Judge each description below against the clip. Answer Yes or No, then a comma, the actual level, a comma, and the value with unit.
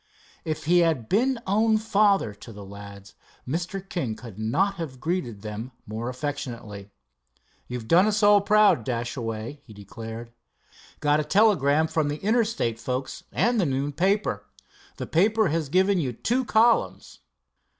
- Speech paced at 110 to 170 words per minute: Yes, average, 150 wpm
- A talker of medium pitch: Yes, medium, 150 Hz